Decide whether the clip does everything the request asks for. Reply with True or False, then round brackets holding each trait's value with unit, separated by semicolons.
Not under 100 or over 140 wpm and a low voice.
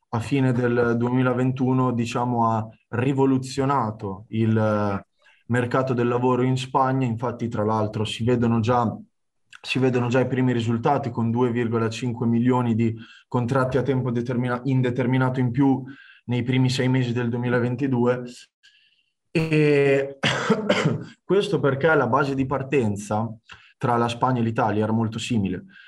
True (130 wpm; 125 Hz)